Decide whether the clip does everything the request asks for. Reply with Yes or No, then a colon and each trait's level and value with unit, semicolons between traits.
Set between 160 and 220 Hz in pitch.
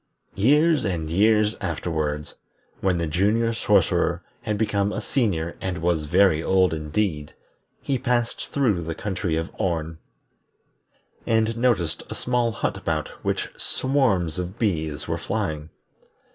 No: very low, 95 Hz